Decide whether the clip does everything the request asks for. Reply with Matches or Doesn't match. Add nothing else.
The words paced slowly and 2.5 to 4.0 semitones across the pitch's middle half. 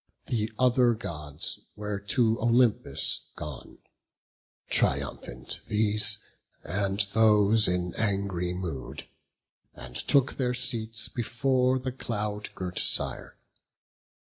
Matches